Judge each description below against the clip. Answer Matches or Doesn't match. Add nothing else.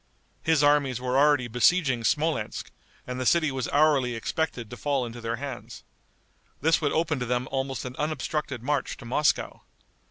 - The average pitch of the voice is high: Doesn't match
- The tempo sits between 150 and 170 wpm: Matches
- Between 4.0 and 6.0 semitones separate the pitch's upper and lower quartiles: Doesn't match